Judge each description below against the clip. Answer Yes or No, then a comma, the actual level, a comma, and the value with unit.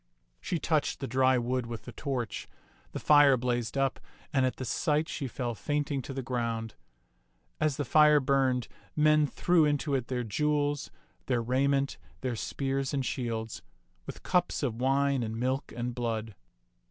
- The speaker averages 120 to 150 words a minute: No, average, 165 wpm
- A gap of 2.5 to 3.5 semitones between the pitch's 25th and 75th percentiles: Yes, average, 3.0 semitones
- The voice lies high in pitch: No, low, 130 Hz